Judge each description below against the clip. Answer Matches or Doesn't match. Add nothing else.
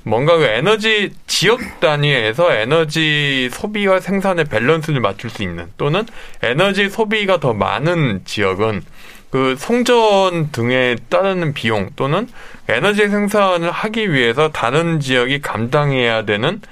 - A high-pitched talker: Doesn't match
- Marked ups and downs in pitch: Matches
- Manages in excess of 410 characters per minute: Doesn't match